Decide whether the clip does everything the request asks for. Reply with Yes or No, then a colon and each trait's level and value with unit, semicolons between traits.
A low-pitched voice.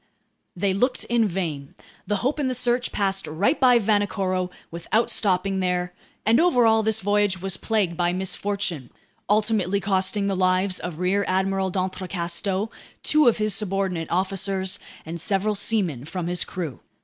No: high, 195 Hz